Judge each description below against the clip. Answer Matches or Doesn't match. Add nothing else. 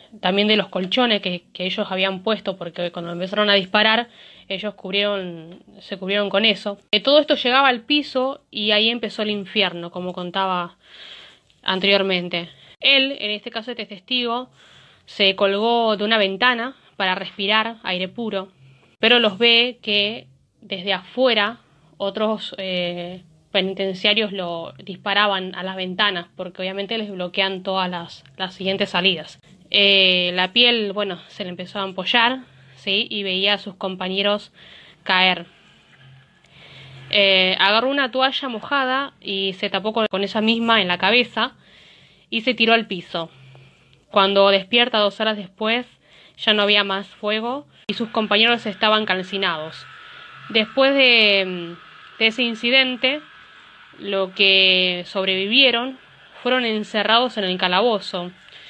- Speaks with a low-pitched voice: Doesn't match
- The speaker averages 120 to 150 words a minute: Matches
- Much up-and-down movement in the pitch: Doesn't match